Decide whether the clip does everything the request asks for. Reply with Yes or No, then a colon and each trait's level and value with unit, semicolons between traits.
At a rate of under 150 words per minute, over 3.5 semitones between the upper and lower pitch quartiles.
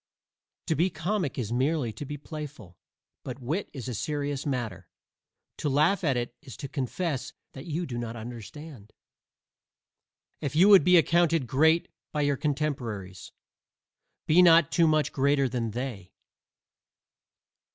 Yes: average, 140 wpm; average, 4.7 semitones